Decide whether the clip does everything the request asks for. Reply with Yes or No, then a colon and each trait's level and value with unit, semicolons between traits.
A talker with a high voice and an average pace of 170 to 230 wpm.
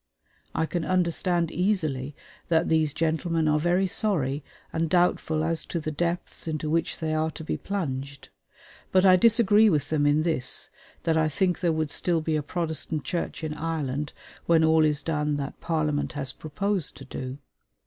No: medium, 160 Hz; average, 175 wpm